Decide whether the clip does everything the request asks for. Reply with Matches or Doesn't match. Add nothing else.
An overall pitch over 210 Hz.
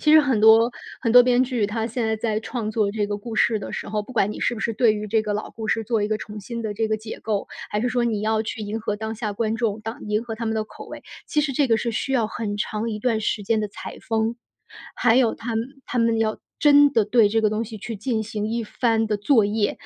Matches